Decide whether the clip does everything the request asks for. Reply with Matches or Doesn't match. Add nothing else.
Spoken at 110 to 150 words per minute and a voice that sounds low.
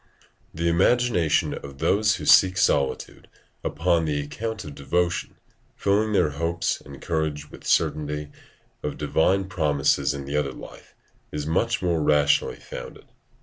Matches